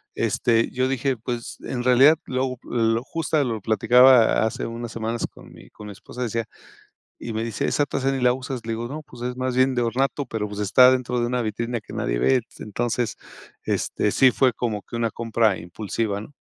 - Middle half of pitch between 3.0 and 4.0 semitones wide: No, narrow, 2.4 semitones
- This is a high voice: No, low, 120 Hz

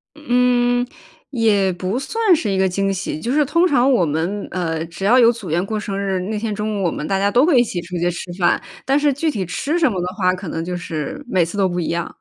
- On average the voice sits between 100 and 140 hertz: No, high, 200 Hz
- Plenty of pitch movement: Yes, wide, 5.7 semitones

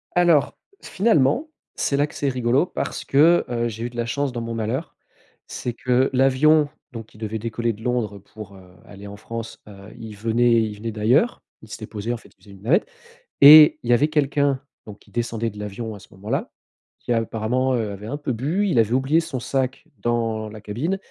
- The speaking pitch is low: Yes, low, 120 Hz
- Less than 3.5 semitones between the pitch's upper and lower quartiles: No, average, 4.2 semitones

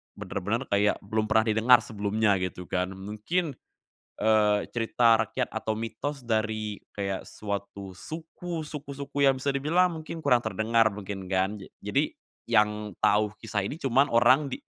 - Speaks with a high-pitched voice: No, low, 110 Hz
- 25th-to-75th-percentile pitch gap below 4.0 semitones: No, average, 4.5 semitones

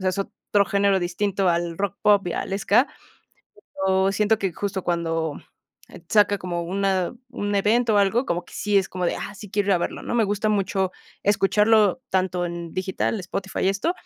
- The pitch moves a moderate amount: No, narrow, 2.2 semitones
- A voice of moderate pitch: No, high, 195 Hz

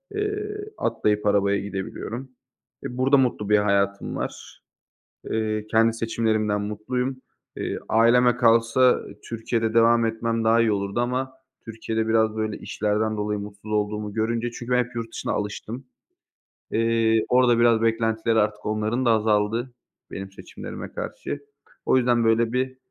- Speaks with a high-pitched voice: No, low, 115 Hz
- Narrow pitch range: Yes, narrow, 2.1 semitones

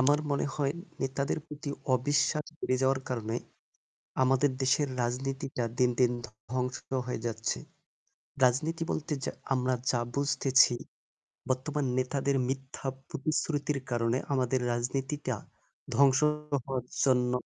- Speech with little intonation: Yes, narrow, 2.0 semitones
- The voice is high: No, low, 130 Hz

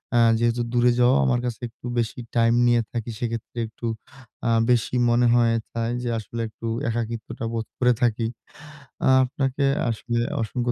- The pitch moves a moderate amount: No, narrow, 1.1 semitones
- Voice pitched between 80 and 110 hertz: No, low, 120 Hz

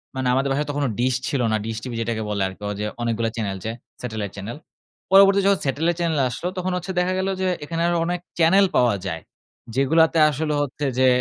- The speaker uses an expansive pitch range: Yes, wide, 6.7 semitones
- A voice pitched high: No, medium, 140 Hz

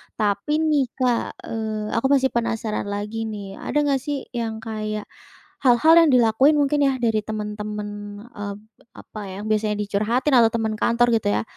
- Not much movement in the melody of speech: No, average, 3.7 semitones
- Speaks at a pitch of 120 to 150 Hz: No, high, 225 Hz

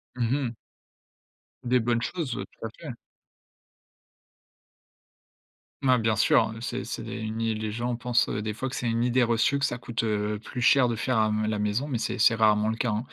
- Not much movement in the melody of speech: Yes, narrow, 2.1 semitones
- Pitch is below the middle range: Yes, low, 115 Hz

